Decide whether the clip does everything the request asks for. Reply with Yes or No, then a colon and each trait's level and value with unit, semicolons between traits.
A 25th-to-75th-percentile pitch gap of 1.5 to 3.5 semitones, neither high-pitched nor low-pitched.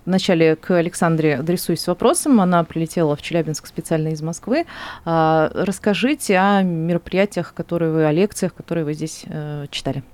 Yes: average, 2.9 semitones; medium, 170 Hz